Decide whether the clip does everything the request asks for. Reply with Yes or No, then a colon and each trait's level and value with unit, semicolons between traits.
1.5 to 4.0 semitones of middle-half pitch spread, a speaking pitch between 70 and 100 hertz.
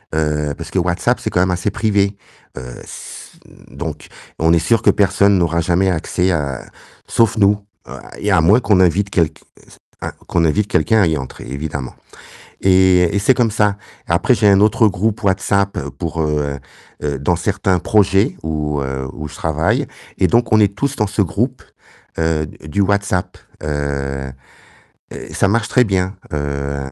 No: average, 4.7 semitones; very low, 90 Hz